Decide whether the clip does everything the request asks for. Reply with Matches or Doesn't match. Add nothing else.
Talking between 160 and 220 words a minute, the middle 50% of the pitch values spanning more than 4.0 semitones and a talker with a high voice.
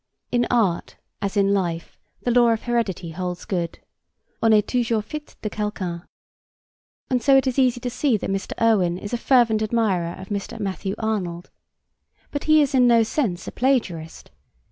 Matches